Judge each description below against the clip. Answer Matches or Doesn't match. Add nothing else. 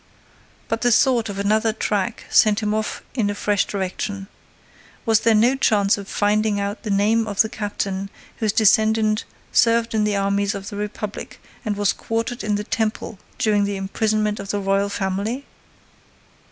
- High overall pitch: Matches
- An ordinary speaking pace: Matches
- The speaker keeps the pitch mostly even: Matches